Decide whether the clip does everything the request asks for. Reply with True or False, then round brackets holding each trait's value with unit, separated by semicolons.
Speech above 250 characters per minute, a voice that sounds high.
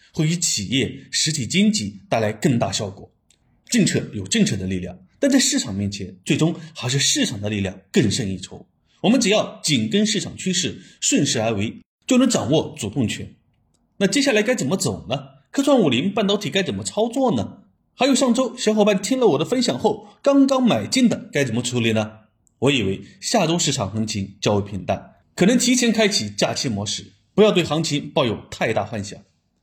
False (290 characters per minute; 170 Hz)